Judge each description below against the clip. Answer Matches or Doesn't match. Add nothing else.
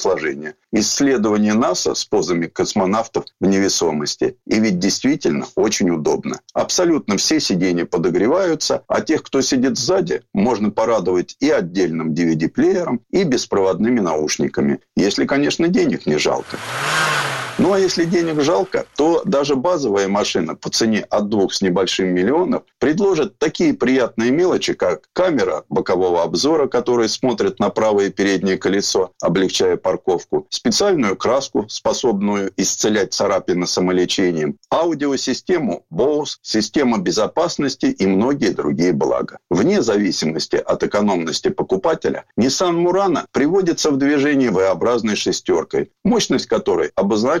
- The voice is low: Matches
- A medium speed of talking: Matches